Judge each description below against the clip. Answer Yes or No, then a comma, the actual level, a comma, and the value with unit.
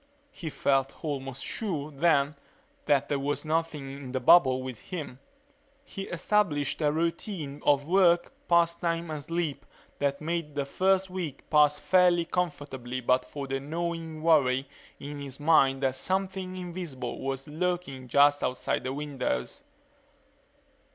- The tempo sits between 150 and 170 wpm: No, average, 140 wpm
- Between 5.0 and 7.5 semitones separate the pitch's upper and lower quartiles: No, average, 3.9 semitones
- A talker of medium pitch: Yes, medium, 150 Hz